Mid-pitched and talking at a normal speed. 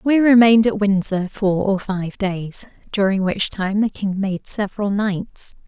No: high, 200 Hz; average, 170 wpm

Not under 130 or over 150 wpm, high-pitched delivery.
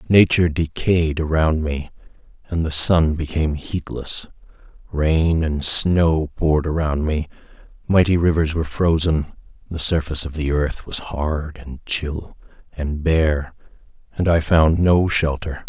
No: slow, 135 wpm; very low, 80 Hz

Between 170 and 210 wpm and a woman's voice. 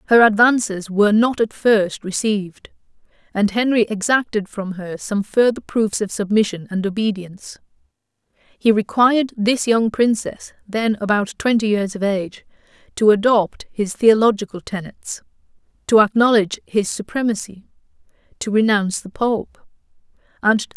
No: average, 155 wpm; female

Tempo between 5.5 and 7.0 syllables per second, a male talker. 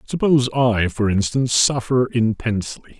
No: 4.9 syllables/s; male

